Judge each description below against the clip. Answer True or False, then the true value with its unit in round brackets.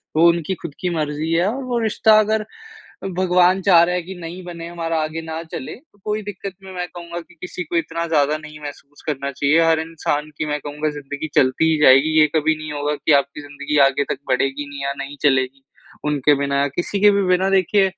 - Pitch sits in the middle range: True (160 Hz)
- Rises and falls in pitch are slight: False (3.6 semitones)